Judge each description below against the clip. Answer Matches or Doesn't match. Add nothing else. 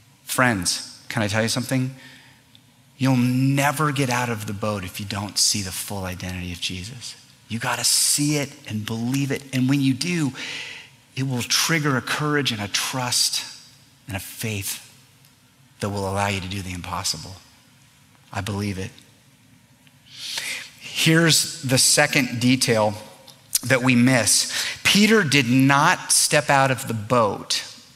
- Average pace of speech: Matches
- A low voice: Matches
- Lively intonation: Doesn't match